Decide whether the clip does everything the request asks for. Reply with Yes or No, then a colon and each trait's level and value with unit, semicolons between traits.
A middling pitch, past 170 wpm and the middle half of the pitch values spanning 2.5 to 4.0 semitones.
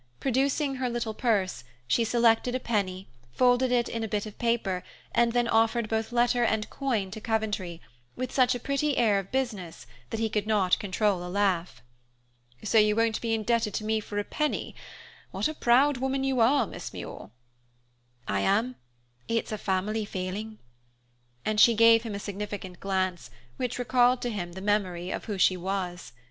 No: high, 220 Hz; average, 180 wpm; average, 3.6 semitones